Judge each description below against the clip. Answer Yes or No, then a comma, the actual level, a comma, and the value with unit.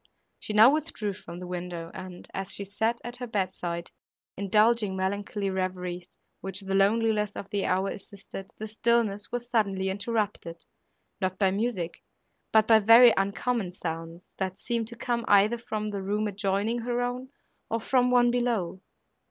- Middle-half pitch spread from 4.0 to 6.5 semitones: No, average, 3.4 semitones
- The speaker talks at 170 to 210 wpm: No, average, 160 wpm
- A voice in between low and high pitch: No, high, 205 Hz